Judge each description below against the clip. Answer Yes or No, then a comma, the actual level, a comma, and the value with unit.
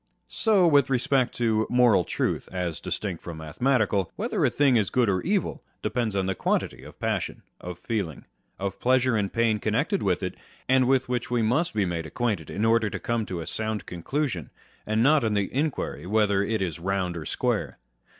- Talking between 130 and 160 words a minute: No, average, 195 wpm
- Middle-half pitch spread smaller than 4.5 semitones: No, average, 4.8 semitones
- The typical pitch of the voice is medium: No, low, 110 Hz